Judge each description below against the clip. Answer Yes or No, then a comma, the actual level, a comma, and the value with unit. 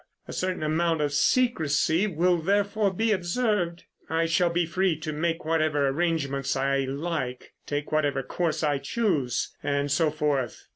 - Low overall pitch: No, medium, 160 Hz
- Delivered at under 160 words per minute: Yes, average, 150 wpm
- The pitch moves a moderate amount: Yes, average, 3.5 semitones